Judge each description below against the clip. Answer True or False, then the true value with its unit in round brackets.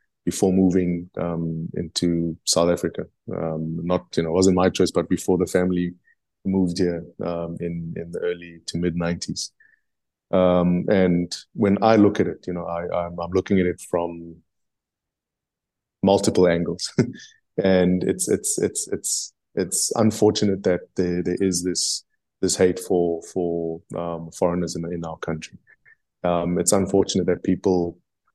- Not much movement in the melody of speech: True (1.6 semitones)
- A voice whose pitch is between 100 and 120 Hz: False (90 Hz)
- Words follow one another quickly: False (155 wpm)